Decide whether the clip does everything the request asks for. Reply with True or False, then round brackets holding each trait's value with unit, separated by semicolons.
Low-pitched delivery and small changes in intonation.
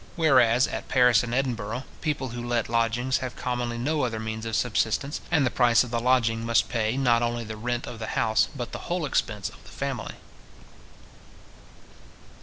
True (120 Hz; 2.0 semitones)